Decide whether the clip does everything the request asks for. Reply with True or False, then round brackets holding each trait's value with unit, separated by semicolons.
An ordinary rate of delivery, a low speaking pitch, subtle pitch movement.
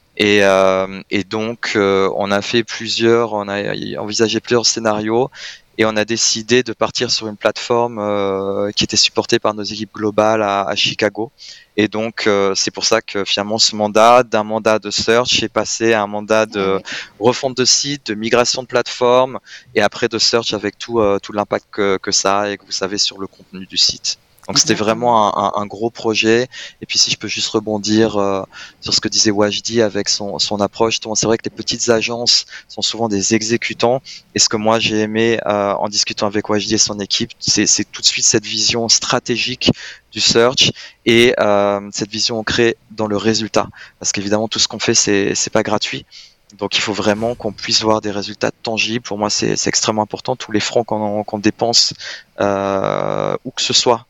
True (205 wpm; 110 Hz; 2.1 semitones)